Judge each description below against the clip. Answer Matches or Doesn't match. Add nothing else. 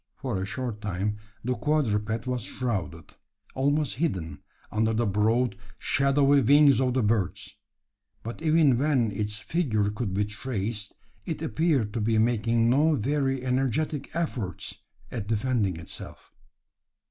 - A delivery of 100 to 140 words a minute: Matches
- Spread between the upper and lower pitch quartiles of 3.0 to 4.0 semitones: Doesn't match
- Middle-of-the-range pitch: Doesn't match